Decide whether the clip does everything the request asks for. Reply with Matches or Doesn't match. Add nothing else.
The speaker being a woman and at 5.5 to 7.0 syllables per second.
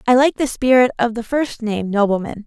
Matches